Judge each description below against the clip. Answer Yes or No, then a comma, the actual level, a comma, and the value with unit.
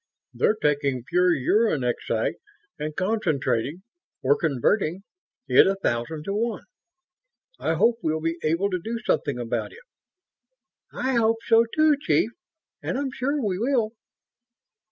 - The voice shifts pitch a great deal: Yes, wide, 7.3 semitones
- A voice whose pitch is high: No, medium, 180 Hz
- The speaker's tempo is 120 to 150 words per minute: Yes, slow, 135 wpm